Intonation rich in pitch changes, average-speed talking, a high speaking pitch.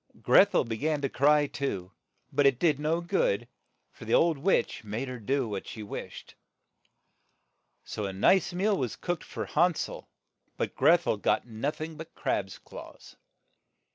No: wide, 6.4 semitones; average, 170 wpm; medium, 140 Hz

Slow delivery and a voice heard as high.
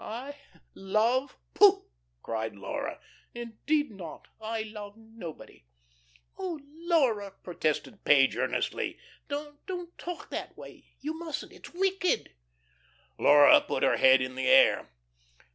Yes: slow, 120 wpm; high, 225 Hz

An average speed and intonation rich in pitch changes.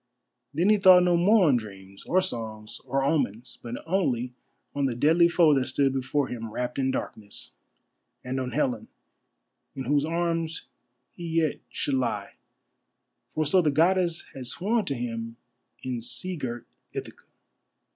Yes: average, 155 wpm; wide, 5.7 semitones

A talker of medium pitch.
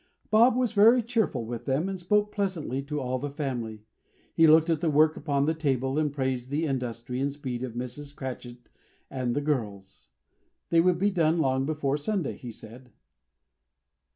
Yes: medium, 145 Hz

